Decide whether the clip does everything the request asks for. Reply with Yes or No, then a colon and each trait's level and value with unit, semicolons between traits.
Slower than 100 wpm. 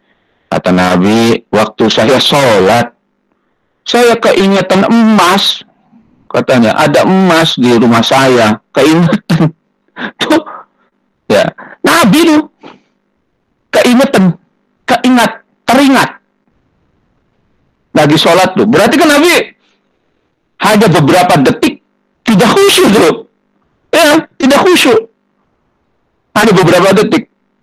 Yes: slow, 85 wpm